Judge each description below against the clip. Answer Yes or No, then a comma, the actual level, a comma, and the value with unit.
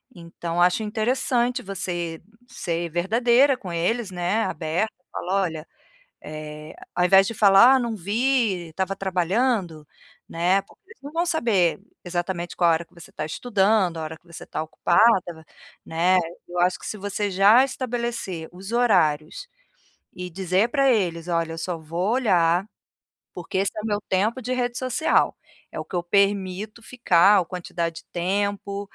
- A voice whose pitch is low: No, high, 190 Hz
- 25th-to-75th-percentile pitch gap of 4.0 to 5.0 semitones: Yes, average, 4.6 semitones